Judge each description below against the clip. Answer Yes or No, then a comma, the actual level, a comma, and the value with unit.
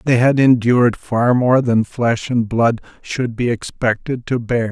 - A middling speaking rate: Yes, average, 180 wpm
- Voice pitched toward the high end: No, low, 120 Hz